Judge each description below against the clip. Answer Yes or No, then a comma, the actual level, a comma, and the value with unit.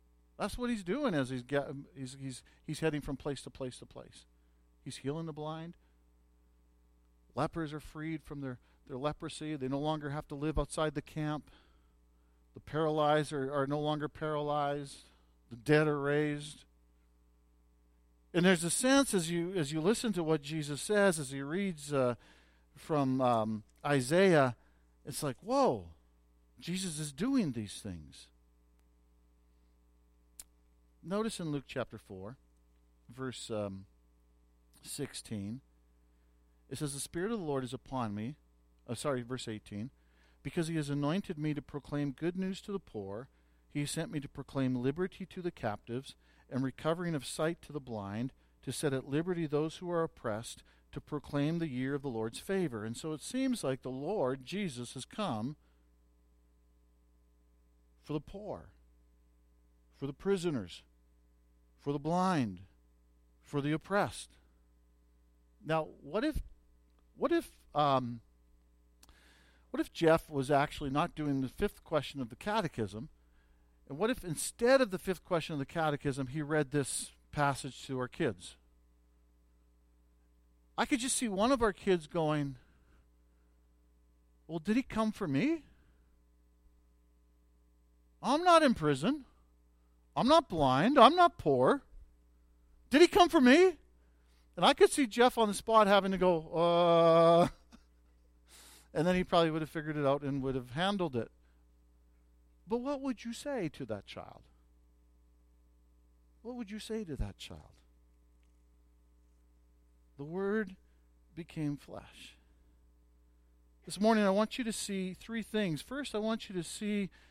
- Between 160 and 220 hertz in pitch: No, low, 130 Hz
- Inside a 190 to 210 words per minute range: No, average, 150 wpm